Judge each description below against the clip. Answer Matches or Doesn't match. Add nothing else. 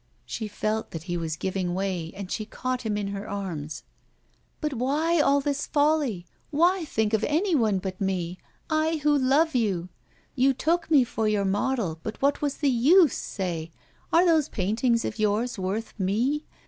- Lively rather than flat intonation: Matches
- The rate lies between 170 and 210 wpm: Matches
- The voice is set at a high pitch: Matches